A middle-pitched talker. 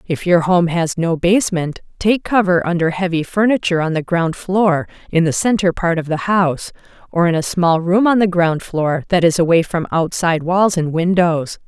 Yes: medium, 175 Hz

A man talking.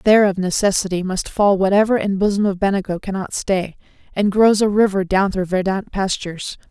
No: female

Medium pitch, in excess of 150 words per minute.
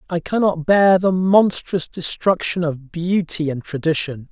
No: medium, 170 Hz; average, 140 wpm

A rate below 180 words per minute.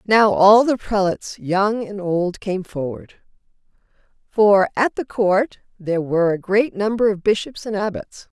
Yes: average, 155 wpm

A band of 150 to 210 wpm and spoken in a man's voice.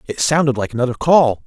Yes: fast, 205 wpm; male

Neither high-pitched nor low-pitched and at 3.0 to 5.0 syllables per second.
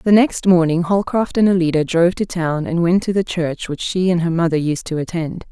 No: medium, 175 Hz; 5.3 syllables/s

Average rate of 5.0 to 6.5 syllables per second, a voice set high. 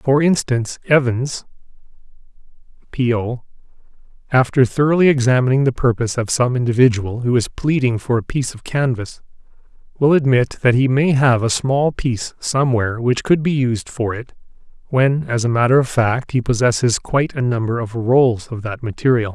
No: 5.3 syllables/s; low, 125 Hz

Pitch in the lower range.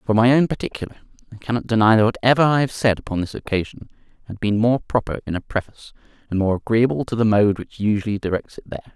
Yes: low, 110 Hz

